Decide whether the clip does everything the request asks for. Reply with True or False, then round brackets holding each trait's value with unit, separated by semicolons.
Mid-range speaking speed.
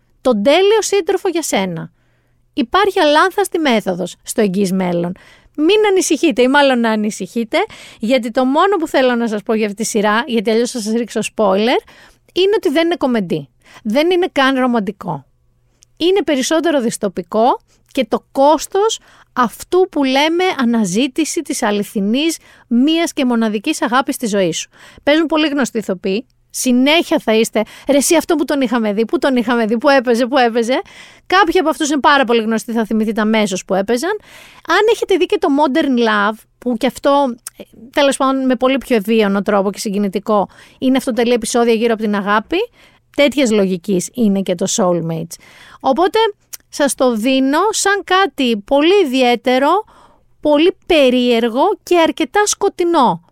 True (160 wpm)